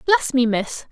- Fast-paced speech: No, average, 195 wpm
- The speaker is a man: No, female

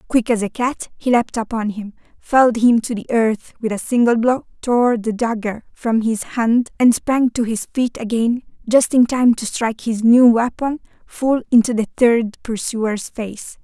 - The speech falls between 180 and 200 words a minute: Yes, average, 190 wpm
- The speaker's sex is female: Yes, female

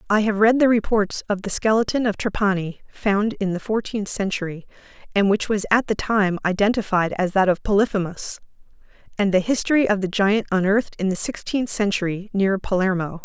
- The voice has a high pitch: Yes, high, 205 Hz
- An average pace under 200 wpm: Yes, average, 175 wpm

